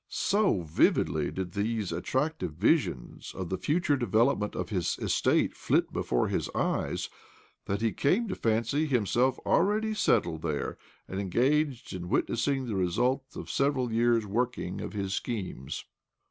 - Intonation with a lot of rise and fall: Yes, wide, 6.4 semitones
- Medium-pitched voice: No, low, 115 Hz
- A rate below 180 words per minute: Yes, average, 145 wpm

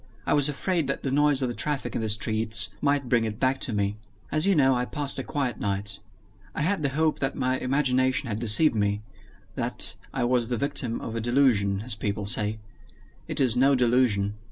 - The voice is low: Yes, low, 125 Hz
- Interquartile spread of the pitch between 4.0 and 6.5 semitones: Yes, average, 4.3 semitones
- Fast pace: Yes, fast, 210 wpm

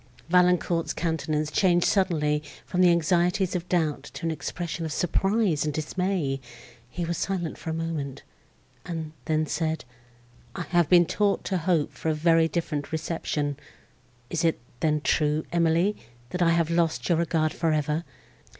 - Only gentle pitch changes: Yes, narrow, 2.2 semitones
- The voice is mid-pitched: Yes, medium, 165 Hz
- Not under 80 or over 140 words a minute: No, average, 155 wpm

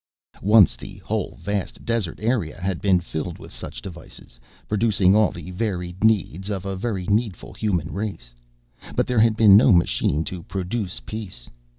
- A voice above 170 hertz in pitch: No, very low, 95 Hz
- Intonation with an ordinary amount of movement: Yes, average, 3.4 semitones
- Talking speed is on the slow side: No, average, 165 wpm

